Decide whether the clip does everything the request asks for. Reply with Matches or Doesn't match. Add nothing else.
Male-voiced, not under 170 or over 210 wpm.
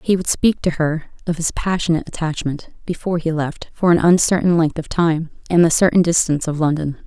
Doesn't match